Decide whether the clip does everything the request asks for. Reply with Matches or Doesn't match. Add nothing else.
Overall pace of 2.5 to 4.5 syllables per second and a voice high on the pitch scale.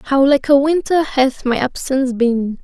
Matches